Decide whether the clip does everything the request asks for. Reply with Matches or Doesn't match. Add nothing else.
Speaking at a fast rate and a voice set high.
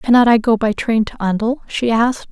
Matches